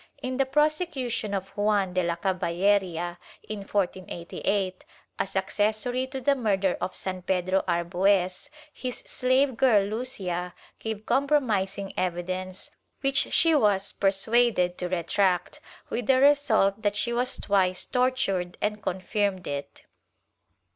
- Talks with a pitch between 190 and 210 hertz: Yes, high, 200 Hz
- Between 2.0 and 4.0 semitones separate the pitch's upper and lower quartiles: No, average, 5.0 semitones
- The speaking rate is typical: No, slow, 125 wpm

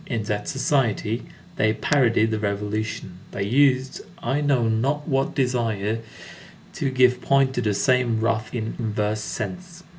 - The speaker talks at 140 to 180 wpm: Yes, average, 145 wpm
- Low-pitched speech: Yes, low, 115 Hz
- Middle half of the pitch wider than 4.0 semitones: No, average, 3.7 semitones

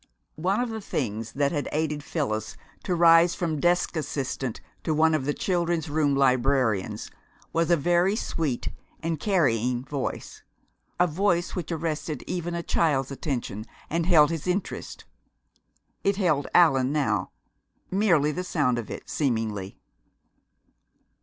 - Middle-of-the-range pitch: Yes, medium, 155 Hz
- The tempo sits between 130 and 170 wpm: Yes, average, 140 wpm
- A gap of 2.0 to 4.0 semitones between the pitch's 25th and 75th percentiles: No, average, 4.5 semitones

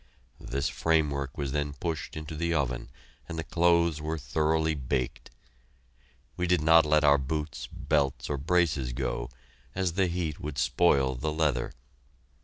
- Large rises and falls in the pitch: No, average, 2.9 semitones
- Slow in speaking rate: No, average, 150 wpm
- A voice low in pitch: Yes, very low, 75 Hz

